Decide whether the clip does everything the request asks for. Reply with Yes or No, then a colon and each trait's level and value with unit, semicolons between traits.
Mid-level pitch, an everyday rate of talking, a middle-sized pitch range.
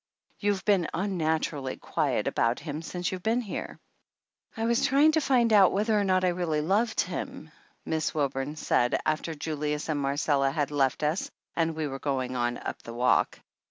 No: medium, 160 Hz; average, 190 wpm; wide, 5.7 semitones